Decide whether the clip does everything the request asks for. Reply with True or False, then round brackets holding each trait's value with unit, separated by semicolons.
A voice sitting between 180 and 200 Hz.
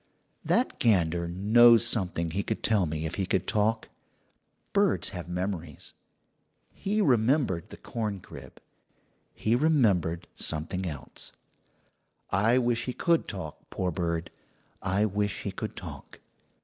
False (100 Hz)